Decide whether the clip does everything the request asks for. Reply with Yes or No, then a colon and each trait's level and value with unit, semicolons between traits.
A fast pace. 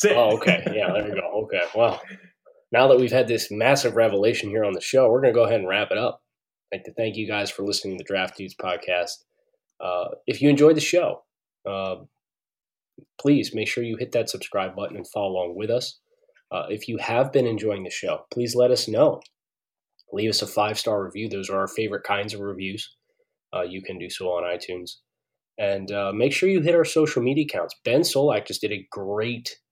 Yes: fast, 220 wpm